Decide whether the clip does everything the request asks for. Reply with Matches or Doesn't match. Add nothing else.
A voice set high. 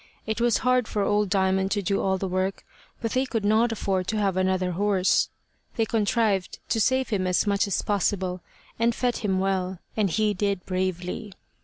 Matches